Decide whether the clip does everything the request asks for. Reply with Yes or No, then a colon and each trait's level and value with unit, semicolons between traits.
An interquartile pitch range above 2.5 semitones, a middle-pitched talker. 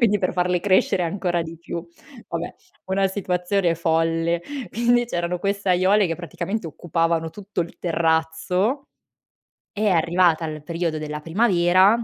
Yes: average, 2.9 semitones; medium, 175 Hz